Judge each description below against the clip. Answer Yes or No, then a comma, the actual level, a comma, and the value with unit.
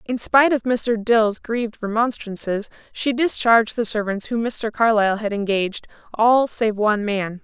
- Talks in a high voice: Yes, high, 220 Hz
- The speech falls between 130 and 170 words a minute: Yes, average, 160 wpm